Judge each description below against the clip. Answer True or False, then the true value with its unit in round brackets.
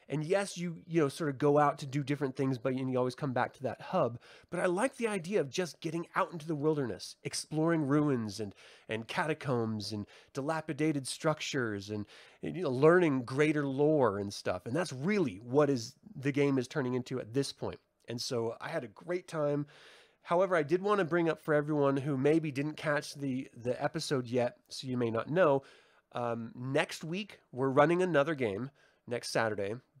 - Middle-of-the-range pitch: True (145 Hz)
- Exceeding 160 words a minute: True (200 wpm)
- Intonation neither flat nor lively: True (4.1 semitones)